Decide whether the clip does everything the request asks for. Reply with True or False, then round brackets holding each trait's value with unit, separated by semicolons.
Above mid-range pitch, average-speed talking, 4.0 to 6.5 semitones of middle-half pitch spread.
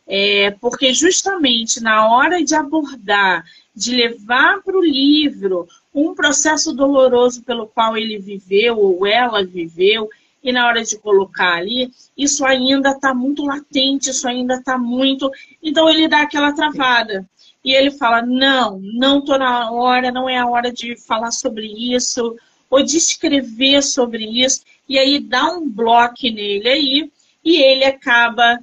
False (260 Hz; 155 wpm; 3.6 semitones)